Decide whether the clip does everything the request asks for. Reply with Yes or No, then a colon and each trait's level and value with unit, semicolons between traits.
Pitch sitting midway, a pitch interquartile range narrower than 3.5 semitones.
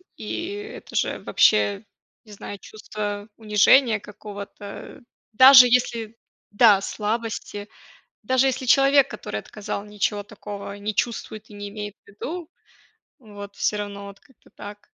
No: high, 210 Hz; average, 2.8 semitones